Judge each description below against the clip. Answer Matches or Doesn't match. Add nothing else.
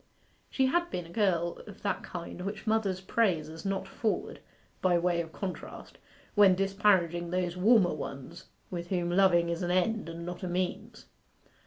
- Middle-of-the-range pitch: Matches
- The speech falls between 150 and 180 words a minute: Matches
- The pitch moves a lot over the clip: Doesn't match